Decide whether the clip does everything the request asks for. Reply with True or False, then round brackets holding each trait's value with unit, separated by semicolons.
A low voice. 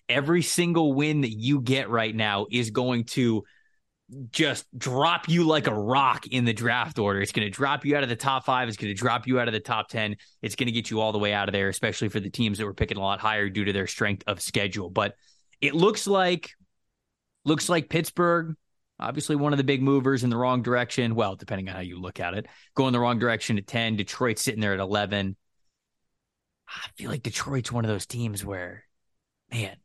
True (120 Hz)